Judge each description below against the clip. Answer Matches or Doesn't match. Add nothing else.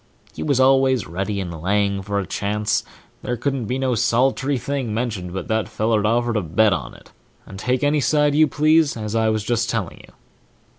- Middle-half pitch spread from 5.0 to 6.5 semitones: Doesn't match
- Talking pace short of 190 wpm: Doesn't match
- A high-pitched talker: Doesn't match